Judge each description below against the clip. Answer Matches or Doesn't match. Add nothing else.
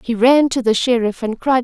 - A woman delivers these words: Matches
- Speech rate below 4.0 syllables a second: Doesn't match